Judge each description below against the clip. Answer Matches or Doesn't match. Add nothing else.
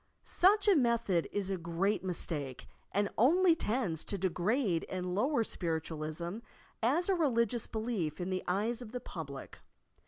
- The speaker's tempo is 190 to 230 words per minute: Doesn't match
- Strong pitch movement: Matches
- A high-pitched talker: Matches